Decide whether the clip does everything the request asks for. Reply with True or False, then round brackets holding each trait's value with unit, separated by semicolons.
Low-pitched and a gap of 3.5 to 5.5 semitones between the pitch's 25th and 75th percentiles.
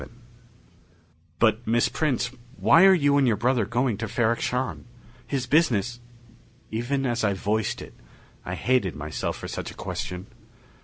False (120 Hz; 3.1 semitones)